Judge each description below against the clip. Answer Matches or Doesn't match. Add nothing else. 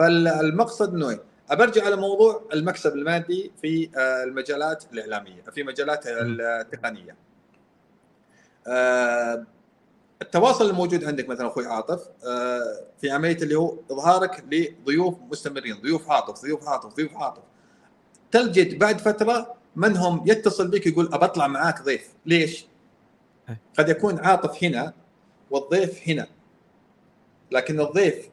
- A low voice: Doesn't match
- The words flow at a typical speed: Matches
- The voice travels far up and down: Matches